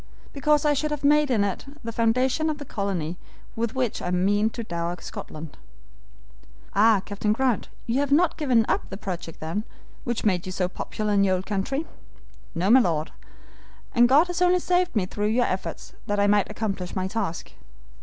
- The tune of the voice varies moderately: No, wide, 5.9 semitones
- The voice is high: Yes, high, 215 Hz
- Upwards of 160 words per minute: Yes, average, 185 wpm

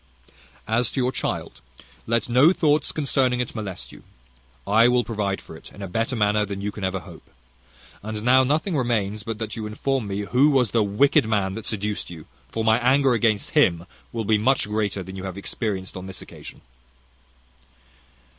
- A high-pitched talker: No, low, 110 Hz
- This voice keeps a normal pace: Yes, average, 190 wpm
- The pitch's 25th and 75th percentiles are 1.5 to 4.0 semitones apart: Yes, average, 3.7 semitones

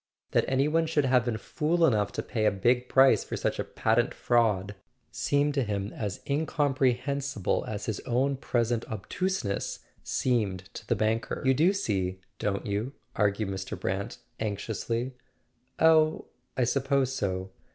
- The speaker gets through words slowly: No, average, 160 wpm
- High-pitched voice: No, low, 120 Hz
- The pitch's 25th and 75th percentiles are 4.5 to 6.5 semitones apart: Yes, average, 5.0 semitones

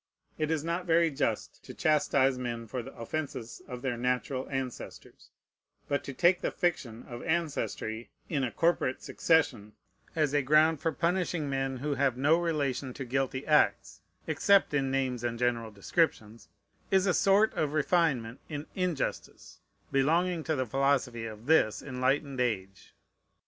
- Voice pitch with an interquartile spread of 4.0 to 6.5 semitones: Yes, average, 4.5 semitones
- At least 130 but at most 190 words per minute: Yes, average, 155 wpm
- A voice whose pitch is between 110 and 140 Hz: Yes, low, 135 Hz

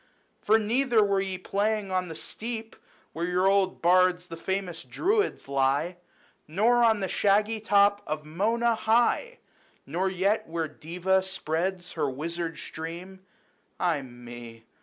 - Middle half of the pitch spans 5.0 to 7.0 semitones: No, average, 4.3 semitones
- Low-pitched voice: No, medium, 185 Hz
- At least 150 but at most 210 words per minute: No, average, 140 wpm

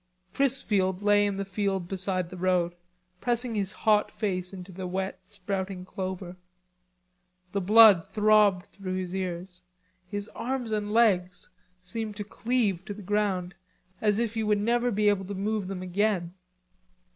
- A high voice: Yes, high, 195 Hz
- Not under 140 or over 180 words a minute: Yes, average, 155 wpm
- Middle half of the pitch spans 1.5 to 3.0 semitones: Yes, narrow, 2.5 semitones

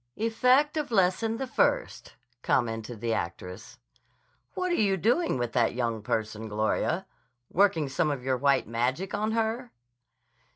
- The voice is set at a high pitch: No, medium, 150 Hz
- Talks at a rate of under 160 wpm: Yes, average, 140 wpm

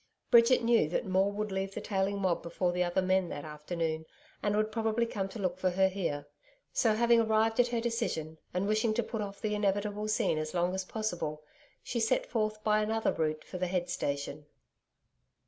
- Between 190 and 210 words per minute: Yes, average, 200 wpm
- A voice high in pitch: Yes, high, 195 Hz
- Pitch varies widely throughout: No, average, 3.7 semitones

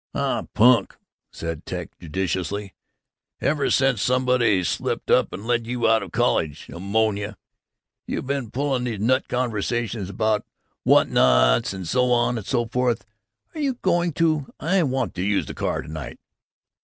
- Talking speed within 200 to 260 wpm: No, average, 155 wpm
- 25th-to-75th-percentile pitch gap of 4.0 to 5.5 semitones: Yes, average, 4.7 semitones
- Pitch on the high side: No, low, 115 Hz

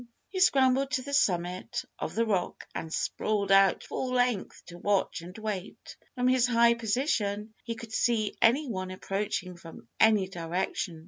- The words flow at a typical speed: Yes, average, 165 wpm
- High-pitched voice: Yes, high, 215 Hz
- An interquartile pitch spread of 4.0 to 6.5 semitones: Yes, average, 4.8 semitones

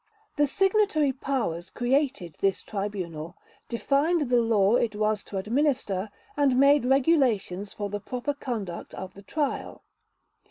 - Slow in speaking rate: Yes, slow, 130 wpm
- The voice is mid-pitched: No, high, 240 Hz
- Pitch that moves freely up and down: Yes, wide, 6.0 semitones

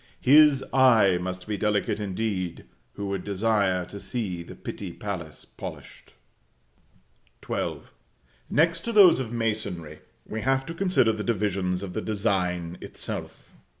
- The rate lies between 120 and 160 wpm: Yes, average, 140 wpm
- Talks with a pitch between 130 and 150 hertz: No, low, 105 Hz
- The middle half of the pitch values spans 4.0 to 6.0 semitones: Yes, average, 4.4 semitones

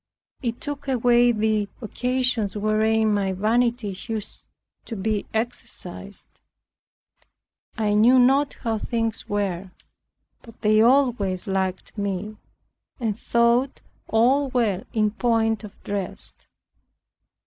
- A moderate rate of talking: No, slow, 105 wpm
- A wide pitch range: No, average, 2.8 semitones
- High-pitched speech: Yes, high, 220 Hz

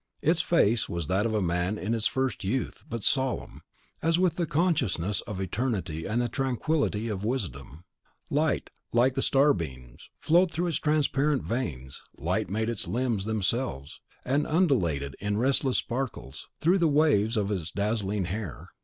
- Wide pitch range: Yes, wide, 6.2 semitones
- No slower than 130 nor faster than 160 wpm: Yes, average, 155 wpm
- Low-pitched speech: Yes, low, 115 Hz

